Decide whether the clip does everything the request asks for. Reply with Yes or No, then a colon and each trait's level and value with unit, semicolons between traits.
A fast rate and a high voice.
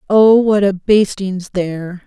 No: average, 145 wpm; high, 195 Hz